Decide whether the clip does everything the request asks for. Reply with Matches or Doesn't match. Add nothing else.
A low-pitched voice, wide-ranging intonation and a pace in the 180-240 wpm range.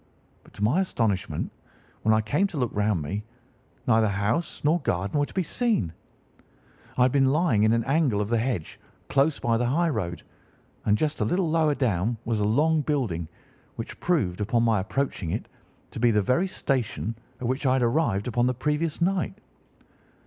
Matches